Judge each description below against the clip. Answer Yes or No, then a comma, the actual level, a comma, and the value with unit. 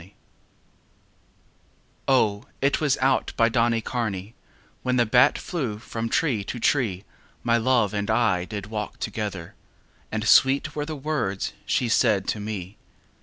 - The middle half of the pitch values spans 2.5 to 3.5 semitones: No, average, 3.9 semitones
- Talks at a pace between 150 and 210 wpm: No, average, 140 wpm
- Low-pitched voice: Yes, low, 115 Hz